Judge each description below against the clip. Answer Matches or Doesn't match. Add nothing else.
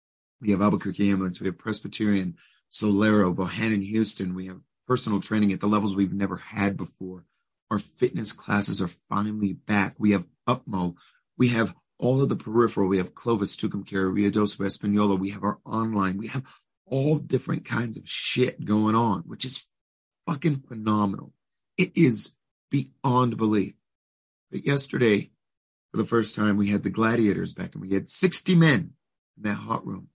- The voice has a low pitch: Matches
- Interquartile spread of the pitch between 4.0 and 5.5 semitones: Doesn't match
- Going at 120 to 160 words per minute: Doesn't match